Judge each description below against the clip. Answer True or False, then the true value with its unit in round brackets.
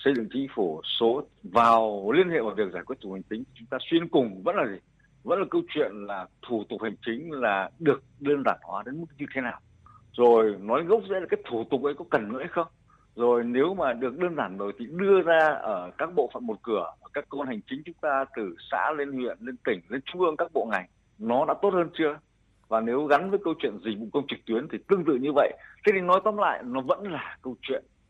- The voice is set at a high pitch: False (135 Hz)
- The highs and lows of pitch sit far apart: True (6.7 semitones)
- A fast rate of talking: True (260 wpm)